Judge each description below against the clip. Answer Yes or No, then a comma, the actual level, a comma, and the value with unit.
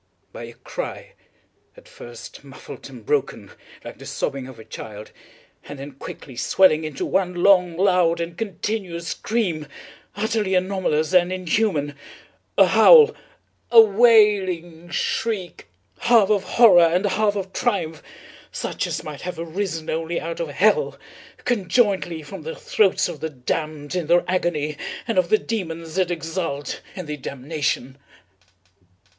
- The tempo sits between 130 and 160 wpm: Yes, average, 140 wpm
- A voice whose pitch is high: No, medium, 175 Hz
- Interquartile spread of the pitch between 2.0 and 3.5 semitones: No, average, 4.4 semitones